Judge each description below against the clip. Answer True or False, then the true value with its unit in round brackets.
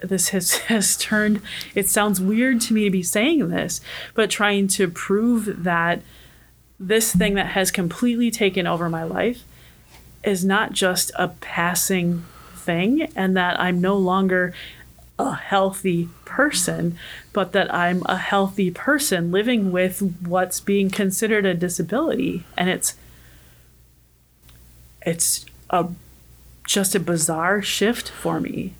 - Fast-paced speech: False (135 wpm)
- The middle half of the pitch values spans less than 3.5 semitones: True (2.9 semitones)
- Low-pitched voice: False (190 Hz)